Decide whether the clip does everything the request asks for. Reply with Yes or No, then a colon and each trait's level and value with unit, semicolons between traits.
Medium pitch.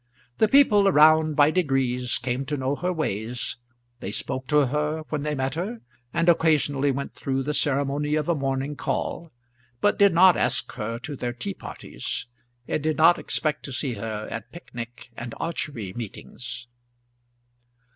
Yes: medium, 145 Hz